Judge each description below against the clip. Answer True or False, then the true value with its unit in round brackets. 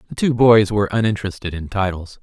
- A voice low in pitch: True (105 Hz)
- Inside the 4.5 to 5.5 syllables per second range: False (6.5 syllables/s)